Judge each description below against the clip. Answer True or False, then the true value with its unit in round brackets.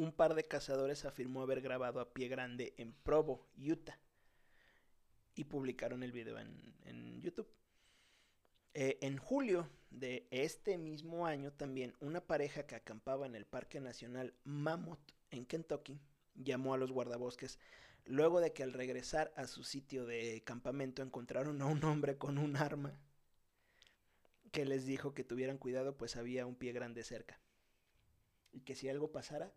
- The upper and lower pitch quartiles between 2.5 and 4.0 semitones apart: True (2.9 semitones)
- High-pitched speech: False (135 Hz)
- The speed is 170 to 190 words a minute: False (155 wpm)